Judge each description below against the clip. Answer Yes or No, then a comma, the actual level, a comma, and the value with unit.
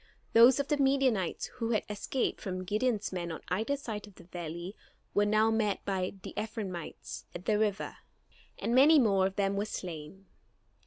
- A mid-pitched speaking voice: No, high, 205 Hz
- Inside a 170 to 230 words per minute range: Yes, average, 175 wpm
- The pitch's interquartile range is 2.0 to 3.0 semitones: No, average, 3.6 semitones